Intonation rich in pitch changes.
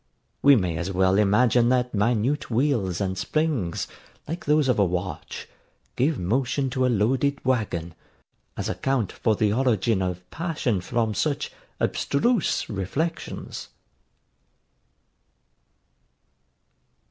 Yes: wide, 6.0 semitones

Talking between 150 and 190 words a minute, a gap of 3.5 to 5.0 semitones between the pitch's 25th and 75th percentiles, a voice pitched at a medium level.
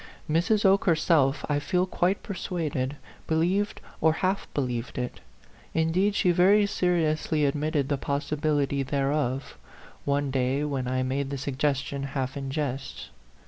Yes: average, 155 wpm; average, 3.8 semitones; medium, 145 Hz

